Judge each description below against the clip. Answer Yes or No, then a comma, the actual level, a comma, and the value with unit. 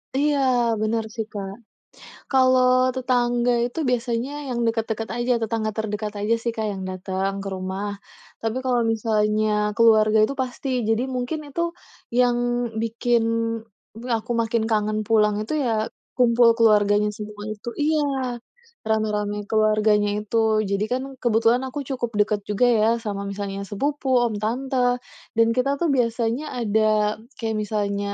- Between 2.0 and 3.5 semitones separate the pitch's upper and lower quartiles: Yes, narrow, 2.6 semitones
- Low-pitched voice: No, high, 225 Hz